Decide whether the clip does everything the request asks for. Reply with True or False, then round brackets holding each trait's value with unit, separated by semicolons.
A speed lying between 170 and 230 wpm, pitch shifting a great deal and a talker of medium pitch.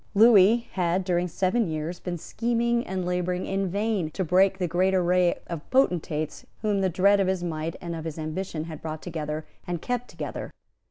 False (185 wpm; 2.9 semitones; 180 Hz)